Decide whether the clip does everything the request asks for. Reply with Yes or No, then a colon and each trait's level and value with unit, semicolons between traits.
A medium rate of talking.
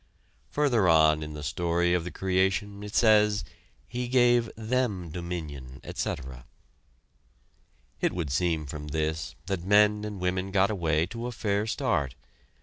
Yes: average, 145 wpm